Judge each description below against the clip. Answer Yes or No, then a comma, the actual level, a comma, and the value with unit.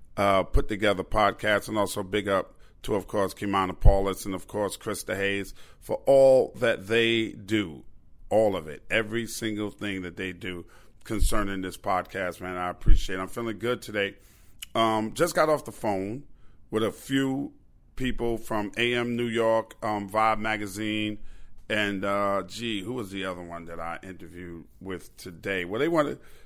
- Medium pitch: No, low, 105 Hz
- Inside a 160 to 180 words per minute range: Yes, average, 170 wpm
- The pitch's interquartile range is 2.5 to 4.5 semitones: Yes, average, 3.1 semitones